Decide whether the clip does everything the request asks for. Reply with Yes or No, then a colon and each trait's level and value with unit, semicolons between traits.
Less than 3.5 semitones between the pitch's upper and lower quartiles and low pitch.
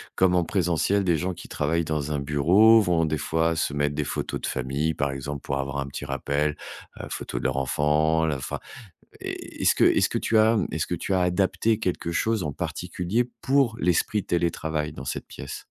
No: average, 4.1 semitones; very low, 80 Hz